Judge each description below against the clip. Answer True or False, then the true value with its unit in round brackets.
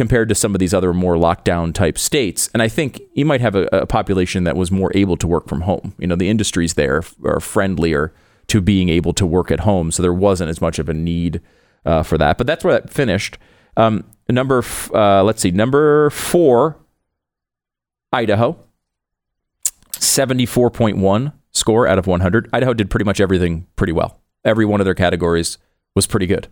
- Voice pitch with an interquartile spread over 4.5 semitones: False (4.2 semitones)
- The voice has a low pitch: True (95 Hz)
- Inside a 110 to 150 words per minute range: False (190 wpm)